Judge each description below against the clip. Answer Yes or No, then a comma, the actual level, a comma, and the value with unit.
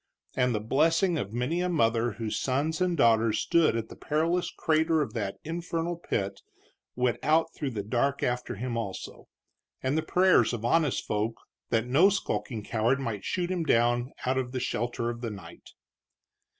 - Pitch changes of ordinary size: No, wide, 5.8 semitones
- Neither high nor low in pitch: No, low, 125 Hz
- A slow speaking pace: No, average, 175 wpm